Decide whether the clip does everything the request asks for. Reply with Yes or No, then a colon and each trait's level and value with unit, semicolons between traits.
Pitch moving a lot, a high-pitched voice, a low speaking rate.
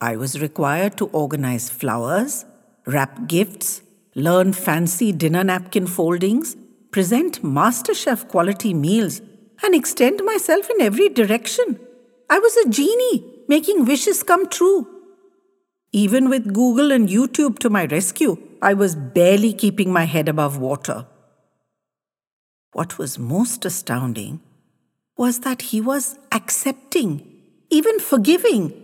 Yes: wide, 7.4 semitones; high, 220 Hz; slow, 120 wpm